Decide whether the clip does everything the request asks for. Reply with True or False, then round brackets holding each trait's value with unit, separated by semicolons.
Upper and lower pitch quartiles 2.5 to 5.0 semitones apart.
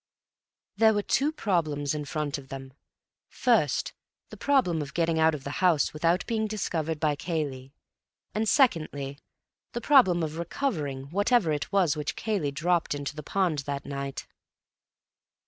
False (5.4 semitones)